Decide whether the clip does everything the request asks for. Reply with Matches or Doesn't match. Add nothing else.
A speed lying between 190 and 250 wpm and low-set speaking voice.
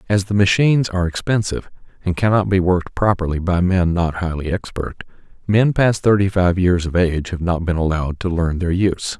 Matches